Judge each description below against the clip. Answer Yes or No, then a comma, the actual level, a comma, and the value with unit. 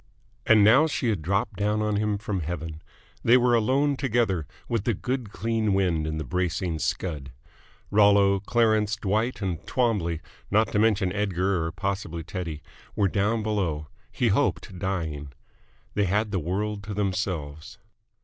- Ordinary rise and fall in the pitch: Yes, average, 3.7 semitones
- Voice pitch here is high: No, low, 100 Hz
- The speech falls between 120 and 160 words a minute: Yes, average, 155 wpm